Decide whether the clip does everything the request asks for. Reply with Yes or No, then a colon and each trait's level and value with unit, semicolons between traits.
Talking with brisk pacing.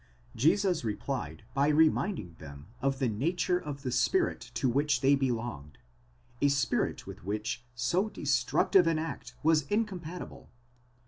No: average, 140 wpm